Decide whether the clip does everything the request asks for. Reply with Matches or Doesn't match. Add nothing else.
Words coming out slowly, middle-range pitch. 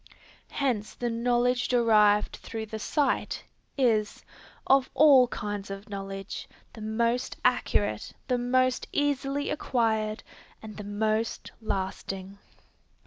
Doesn't match